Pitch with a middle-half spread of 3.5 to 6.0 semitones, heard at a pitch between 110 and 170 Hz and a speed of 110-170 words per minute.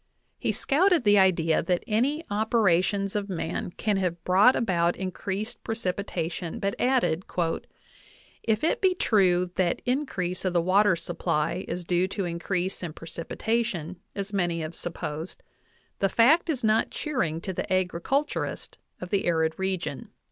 No: average, 4.1 semitones; high, 190 Hz; average, 155 wpm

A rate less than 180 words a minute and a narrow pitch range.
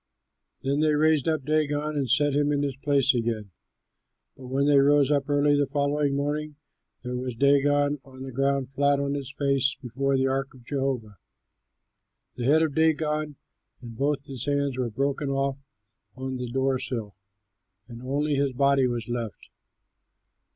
Yes: average, 165 wpm; narrow, 1.8 semitones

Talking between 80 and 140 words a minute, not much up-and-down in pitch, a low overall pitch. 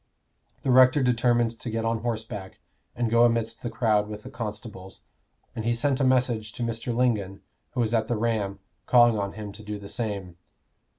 No: average, 190 wpm; narrow, 2.2 semitones; low, 115 Hz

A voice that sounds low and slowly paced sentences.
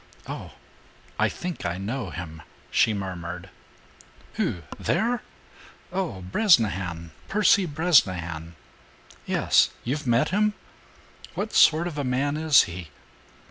Yes: low, 120 Hz; slow, 110 wpm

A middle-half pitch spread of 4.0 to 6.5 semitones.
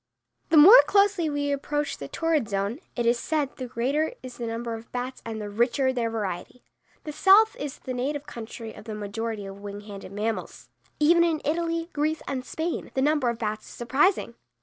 Yes: average, 5.3 semitones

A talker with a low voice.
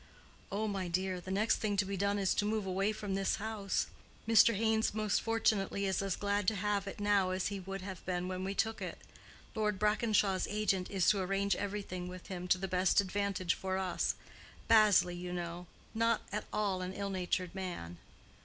No: high, 195 Hz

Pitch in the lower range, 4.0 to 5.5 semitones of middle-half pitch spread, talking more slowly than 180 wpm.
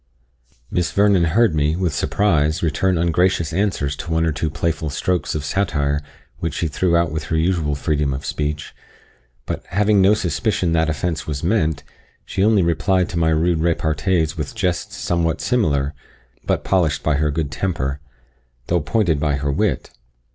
No: very low, 80 Hz; average, 3.4 semitones; average, 170 wpm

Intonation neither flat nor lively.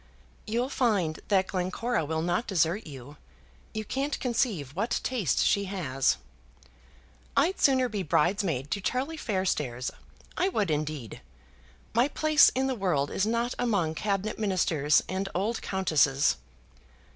No: wide, 7.0 semitones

